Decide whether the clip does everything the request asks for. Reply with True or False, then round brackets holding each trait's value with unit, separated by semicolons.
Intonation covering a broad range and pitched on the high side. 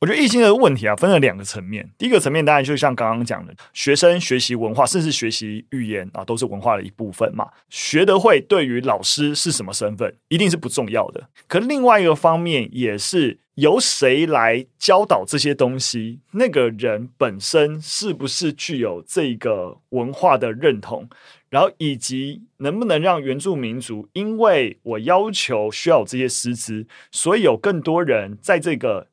False (6.6 semitones; 135 Hz)